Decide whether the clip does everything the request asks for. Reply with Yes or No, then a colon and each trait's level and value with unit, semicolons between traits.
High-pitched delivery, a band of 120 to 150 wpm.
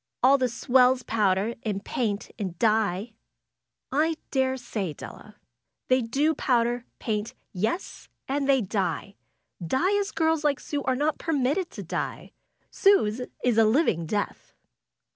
Yes: high, 245 Hz; slow, 135 wpm